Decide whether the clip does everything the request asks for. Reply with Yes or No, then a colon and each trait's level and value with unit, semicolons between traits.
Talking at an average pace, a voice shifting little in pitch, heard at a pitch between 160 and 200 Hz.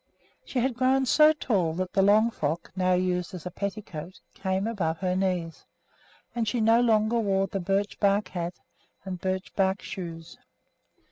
No: average, 165 wpm; average, 3.3 semitones; high, 190 Hz